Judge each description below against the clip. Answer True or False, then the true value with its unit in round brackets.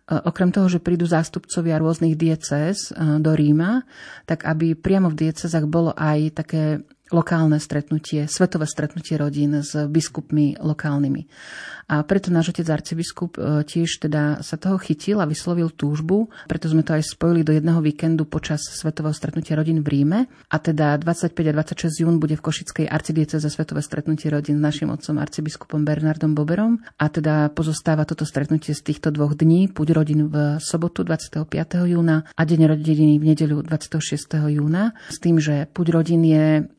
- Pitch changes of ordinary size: False (1.7 semitones)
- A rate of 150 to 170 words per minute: True (165 wpm)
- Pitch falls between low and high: True (155 Hz)